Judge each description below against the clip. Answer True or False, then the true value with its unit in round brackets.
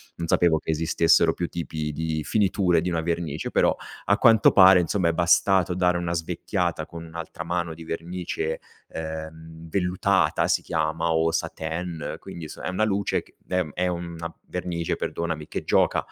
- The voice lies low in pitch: True (85 Hz)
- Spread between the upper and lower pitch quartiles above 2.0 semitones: False (1.7 semitones)